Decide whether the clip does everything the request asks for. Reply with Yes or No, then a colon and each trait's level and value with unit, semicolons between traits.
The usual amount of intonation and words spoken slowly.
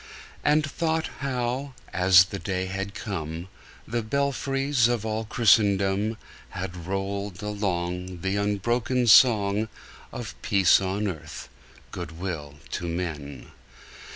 Yes: average, 4.4 semitones; slow, 115 wpm